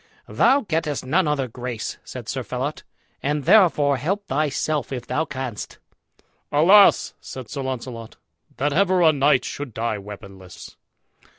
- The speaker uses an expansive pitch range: No, average, 4.3 semitones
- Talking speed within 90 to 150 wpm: Yes, slow, 135 wpm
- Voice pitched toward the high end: No, medium, 140 Hz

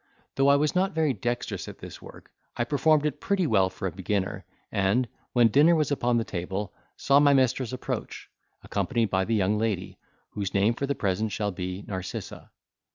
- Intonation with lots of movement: Yes, wide, 6.3 semitones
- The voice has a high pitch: No, low, 115 Hz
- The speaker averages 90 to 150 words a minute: No, average, 190 wpm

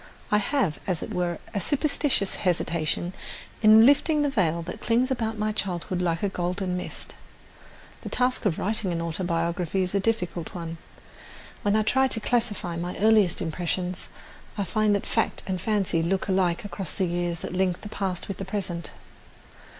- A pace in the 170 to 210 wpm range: Yes, average, 175 wpm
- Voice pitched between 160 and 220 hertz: Yes, high, 190 Hz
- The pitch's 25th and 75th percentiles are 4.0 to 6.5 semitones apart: No, average, 3.6 semitones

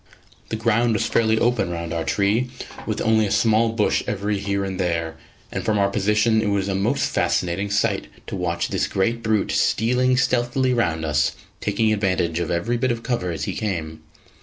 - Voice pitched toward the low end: Yes, low, 105 Hz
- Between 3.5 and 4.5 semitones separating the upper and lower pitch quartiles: Yes, average, 4.0 semitones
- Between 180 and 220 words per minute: Yes, average, 190 wpm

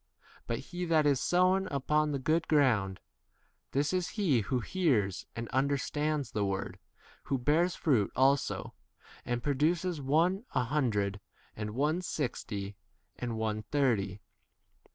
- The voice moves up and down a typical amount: No, wide, 5.8 semitones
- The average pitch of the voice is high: No, medium, 140 Hz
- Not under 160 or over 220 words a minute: No, average, 140 wpm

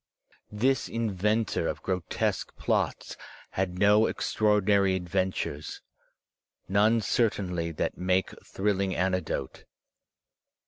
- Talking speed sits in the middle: No, slow, 90 wpm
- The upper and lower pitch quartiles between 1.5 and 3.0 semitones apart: Yes, narrow, 2.4 semitones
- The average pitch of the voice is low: Yes, very low, 95 Hz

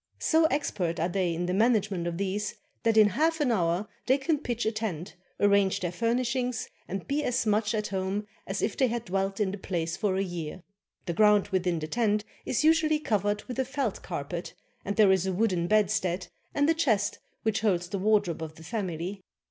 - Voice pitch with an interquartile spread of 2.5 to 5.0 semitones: Yes, average, 4.2 semitones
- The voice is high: Yes, high, 205 Hz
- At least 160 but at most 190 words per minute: No, fast, 205 wpm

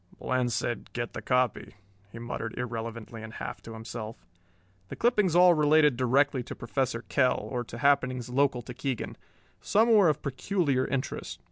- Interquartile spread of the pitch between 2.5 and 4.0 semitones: Yes, average, 3.5 semitones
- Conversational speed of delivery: Yes, average, 160 wpm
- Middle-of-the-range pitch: No, low, 125 Hz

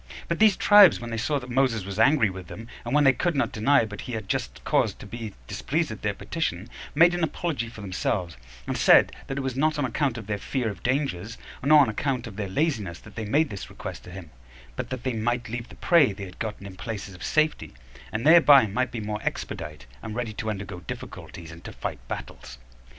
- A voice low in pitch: Yes, low, 115 Hz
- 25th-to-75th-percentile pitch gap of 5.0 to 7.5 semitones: Yes, wide, 5.5 semitones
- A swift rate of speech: Yes, fast, 235 wpm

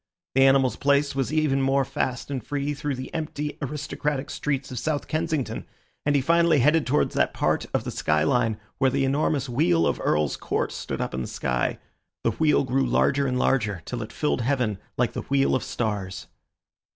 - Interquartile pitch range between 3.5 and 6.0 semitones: No, average, 3.1 semitones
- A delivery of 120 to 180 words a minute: No, average, 195 wpm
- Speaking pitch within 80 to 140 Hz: Yes, low, 135 Hz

